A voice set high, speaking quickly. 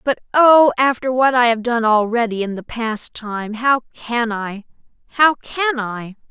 No: high, 240 Hz; average, 170 wpm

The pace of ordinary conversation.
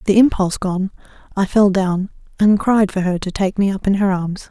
No: fast, 225 wpm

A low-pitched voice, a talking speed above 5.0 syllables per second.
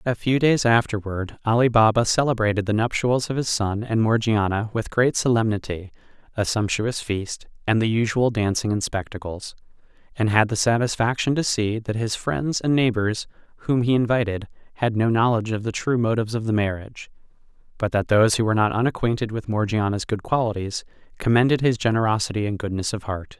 Yes: low, 110 Hz; 5.6 syllables/s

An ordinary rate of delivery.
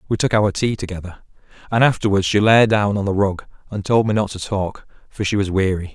No: fast, 230 wpm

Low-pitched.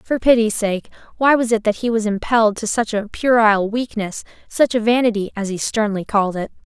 No: high, 220 Hz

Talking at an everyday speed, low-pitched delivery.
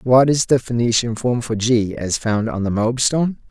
No: fast, 225 wpm; low, 120 Hz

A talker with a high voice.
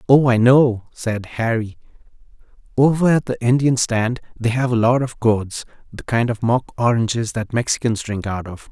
No: low, 120 Hz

